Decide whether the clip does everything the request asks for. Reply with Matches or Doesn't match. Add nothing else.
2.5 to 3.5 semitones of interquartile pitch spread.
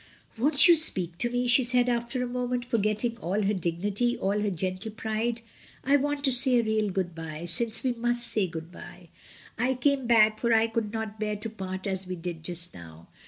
Doesn't match